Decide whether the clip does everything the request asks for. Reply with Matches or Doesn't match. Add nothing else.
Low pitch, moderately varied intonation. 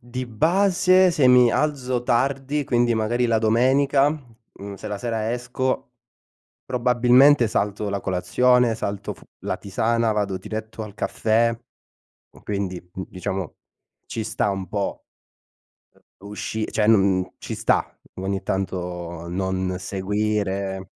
Matches